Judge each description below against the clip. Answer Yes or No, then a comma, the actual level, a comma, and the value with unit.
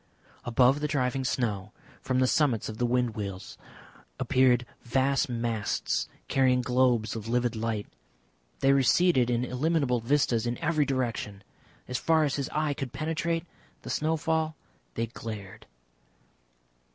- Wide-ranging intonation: No, average, 3.7 semitones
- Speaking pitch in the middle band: No, low, 125 Hz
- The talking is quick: No, slow, 135 wpm